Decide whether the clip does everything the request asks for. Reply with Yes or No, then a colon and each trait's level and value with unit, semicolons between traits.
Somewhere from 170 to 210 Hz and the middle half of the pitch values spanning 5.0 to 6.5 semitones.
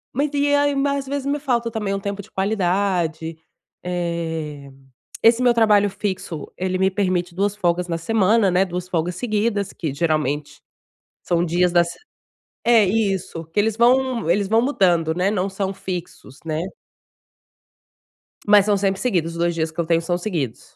No: high, 190 Hz; average, 4.2 semitones